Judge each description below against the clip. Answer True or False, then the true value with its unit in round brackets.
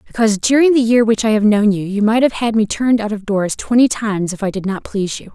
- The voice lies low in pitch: False (215 Hz)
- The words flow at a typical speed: False (290 wpm)